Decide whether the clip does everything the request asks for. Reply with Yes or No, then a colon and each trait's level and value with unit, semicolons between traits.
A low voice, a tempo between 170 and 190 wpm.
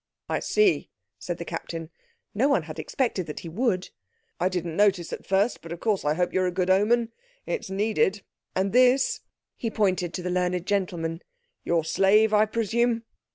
No: high, 195 Hz; average, 180 wpm